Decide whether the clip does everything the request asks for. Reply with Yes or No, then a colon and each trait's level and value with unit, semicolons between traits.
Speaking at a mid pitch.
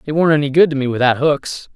Yes: medium, 145 Hz